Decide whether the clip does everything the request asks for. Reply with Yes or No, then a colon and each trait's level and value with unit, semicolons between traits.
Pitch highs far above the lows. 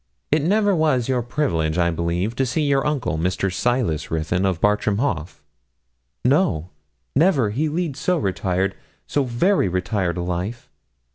Yes: wide, 8.2 semitones